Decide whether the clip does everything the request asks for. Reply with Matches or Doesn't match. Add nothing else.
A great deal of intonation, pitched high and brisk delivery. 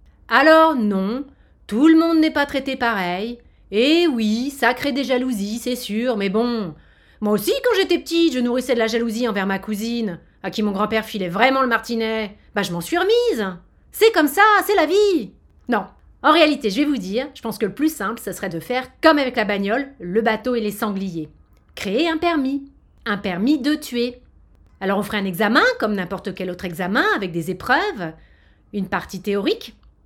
Doesn't match